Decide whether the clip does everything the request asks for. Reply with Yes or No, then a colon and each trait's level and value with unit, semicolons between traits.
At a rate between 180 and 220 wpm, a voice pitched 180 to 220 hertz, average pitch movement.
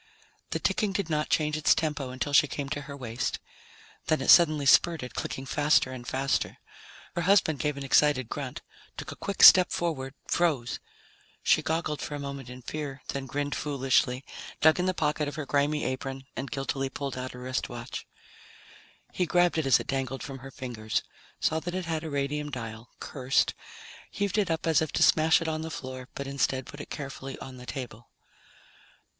No: average, 190 wpm; medium, 140 Hz; average, 3.1 semitones